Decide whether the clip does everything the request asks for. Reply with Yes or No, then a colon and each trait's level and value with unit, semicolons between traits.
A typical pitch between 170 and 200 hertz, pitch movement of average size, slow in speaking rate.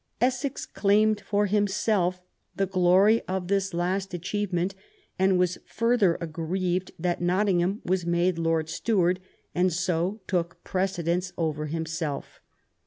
No: medium, 185 Hz; narrow, 2.3 semitones; slow, 120 wpm